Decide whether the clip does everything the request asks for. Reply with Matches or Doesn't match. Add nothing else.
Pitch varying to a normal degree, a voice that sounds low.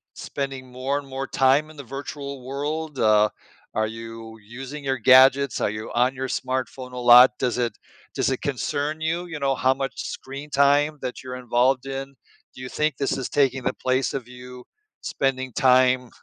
Doesn't match